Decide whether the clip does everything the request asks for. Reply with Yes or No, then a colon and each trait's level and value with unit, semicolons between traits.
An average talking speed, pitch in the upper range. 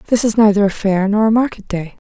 No: fast, 260 wpm; high, 210 Hz